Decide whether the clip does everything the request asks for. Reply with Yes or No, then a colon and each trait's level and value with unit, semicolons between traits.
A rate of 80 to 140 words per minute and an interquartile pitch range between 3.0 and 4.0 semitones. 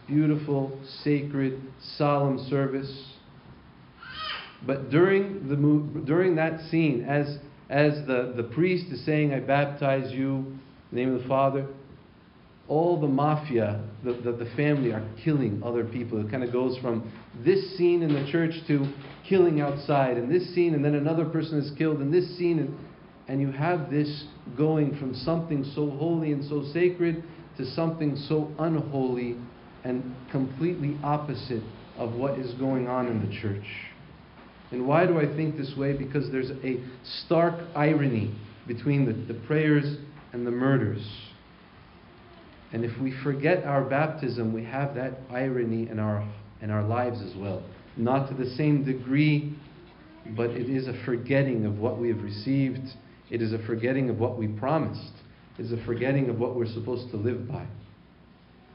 No: average, 165 wpm; average, 3.6 semitones